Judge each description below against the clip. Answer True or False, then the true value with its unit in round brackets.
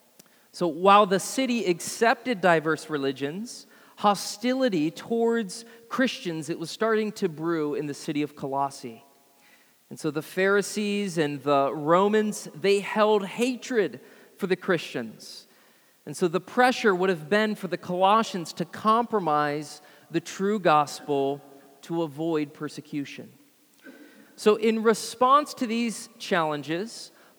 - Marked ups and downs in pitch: True (6.5 semitones)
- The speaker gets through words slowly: True (125 wpm)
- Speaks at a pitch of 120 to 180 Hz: False (190 Hz)